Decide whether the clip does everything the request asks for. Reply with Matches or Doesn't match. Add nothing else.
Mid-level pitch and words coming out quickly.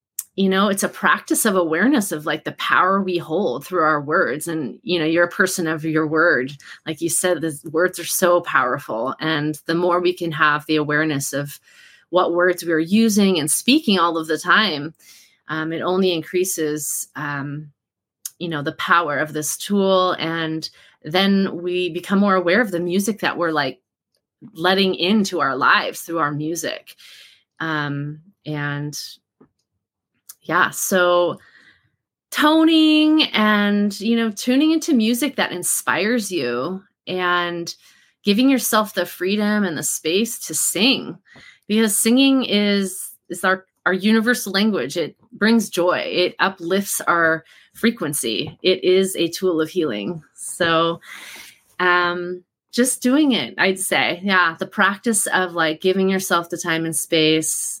Doesn't match